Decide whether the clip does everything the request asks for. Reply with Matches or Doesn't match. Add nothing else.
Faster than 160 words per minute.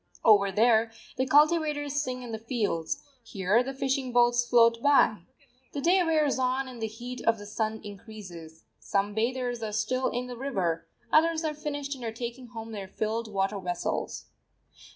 Matches